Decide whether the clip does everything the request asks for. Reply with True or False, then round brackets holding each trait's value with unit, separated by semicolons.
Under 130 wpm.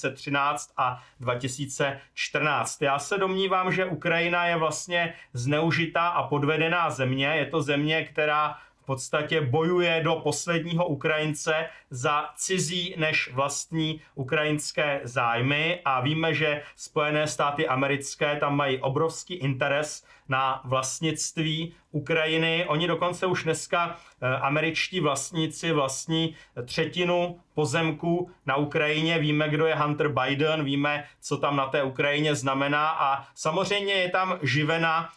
True (120 wpm)